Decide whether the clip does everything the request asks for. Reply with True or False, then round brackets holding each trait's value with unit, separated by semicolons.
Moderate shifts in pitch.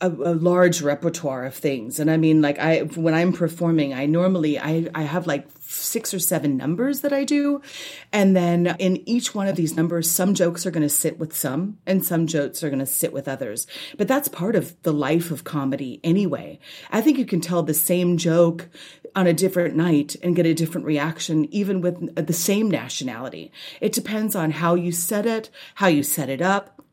True (3.2 semitones)